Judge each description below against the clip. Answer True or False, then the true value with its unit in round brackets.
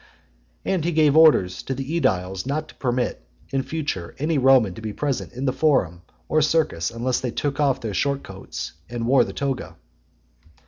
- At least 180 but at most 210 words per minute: True (185 wpm)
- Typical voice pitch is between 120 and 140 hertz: True (135 Hz)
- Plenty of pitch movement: False (4.9 semitones)